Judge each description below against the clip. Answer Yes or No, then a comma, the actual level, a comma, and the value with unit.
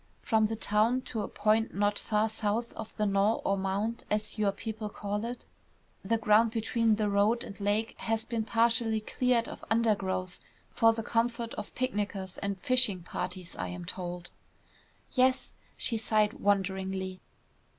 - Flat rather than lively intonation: Yes, narrow, 2.3 semitones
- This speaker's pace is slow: No, average, 160 wpm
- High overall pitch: Yes, high, 215 Hz